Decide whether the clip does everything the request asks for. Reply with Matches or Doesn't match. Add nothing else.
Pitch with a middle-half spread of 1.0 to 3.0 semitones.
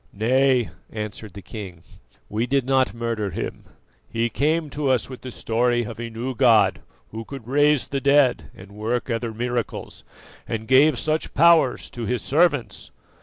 Doesn't match